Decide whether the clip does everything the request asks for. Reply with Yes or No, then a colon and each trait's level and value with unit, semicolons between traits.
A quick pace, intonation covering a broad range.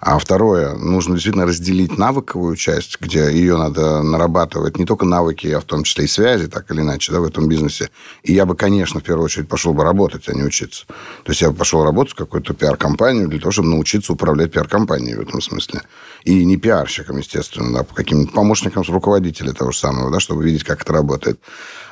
No: fast, 210 wpm; average, 3.2 semitones